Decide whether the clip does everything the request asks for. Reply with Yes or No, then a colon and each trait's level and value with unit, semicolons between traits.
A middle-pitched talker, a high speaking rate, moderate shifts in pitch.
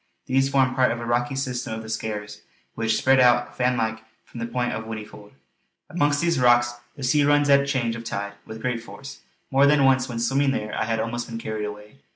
No: low, 120 Hz; fast, 220 wpm; average, 3.1 semitones